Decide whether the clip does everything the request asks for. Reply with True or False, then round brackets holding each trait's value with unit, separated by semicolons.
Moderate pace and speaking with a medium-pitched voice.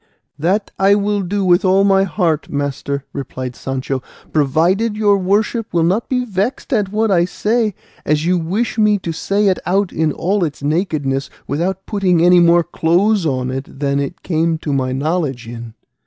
True (180 wpm; 175 Hz)